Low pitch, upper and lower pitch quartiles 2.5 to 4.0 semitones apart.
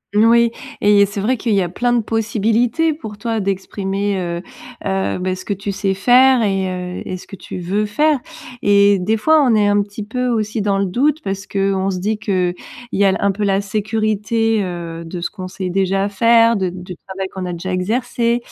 No: high, 200 Hz; average, 2.9 semitones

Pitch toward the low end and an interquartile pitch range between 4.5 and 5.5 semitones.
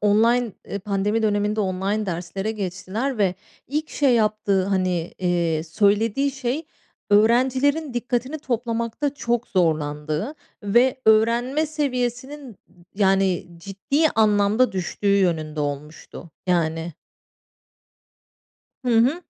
No: high, 210 Hz; average, 4.9 semitones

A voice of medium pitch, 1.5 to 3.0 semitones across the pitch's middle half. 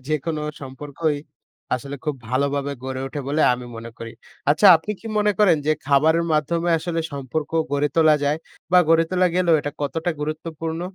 Yes: medium, 155 Hz; average, 2.7 semitones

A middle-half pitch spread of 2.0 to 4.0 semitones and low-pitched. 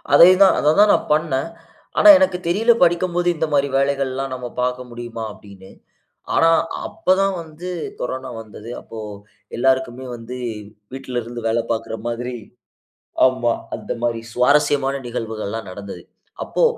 No: average, 4.6 semitones; low, 130 Hz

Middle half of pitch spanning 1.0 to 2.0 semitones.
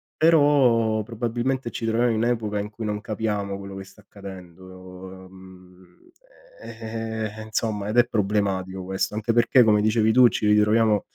No: average, 2.9 semitones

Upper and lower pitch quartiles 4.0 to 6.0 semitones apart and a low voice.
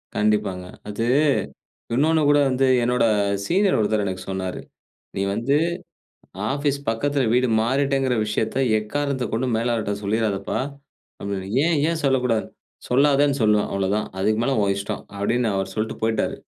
Yes: average, 4.7 semitones; low, 115 Hz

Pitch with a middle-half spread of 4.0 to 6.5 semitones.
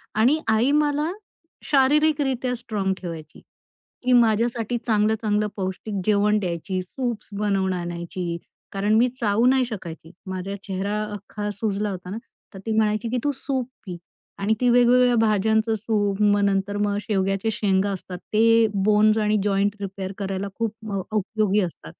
No: average, 2.8 semitones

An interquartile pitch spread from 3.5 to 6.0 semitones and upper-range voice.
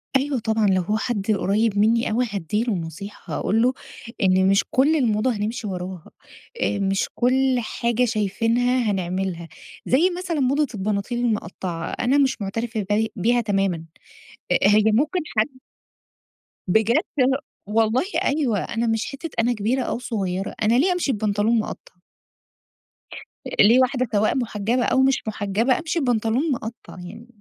Yes: average, 3.8 semitones; high, 225 Hz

